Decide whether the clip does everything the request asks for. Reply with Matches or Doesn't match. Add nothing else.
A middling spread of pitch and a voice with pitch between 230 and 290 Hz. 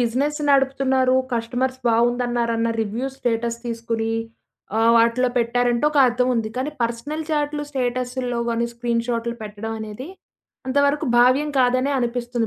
Doesn't match